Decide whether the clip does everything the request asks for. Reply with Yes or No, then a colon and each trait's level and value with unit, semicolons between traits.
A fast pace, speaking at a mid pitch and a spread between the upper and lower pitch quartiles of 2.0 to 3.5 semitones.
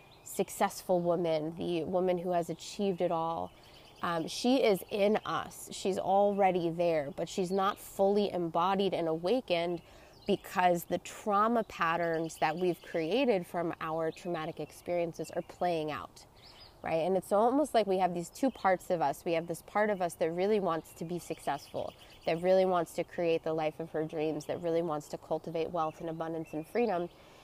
No: average, 180 wpm; medium, 175 Hz; average, 2.8 semitones